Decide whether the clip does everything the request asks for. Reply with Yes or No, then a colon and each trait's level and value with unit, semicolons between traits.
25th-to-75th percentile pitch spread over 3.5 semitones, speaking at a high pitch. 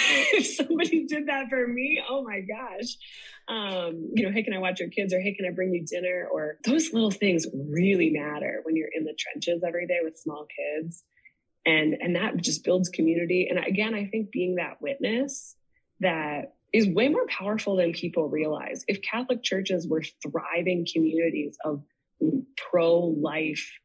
No: wide, 5.5 semitones; medium, 180 Hz